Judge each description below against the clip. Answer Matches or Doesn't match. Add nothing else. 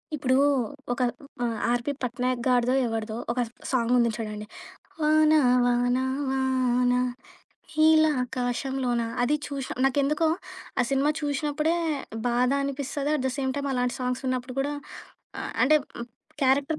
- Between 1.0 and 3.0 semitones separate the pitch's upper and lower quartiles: Matches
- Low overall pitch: Doesn't match